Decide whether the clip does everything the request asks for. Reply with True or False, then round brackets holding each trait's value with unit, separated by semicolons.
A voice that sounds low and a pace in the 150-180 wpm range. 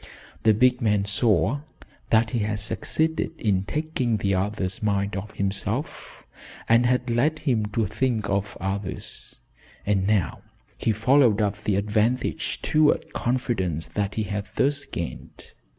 False (110 Hz; 140 wpm)